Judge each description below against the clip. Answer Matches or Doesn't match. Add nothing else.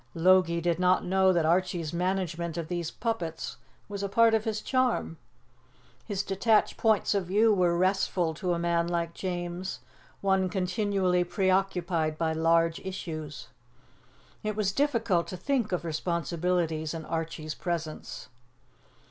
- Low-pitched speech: Doesn't match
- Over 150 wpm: Doesn't match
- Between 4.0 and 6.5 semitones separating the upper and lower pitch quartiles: Doesn't match